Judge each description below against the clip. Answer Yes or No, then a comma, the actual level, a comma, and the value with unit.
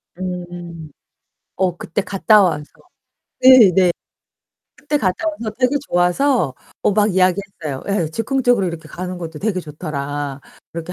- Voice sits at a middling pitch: Yes, medium, 180 Hz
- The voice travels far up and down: No, average, 4.3 semitones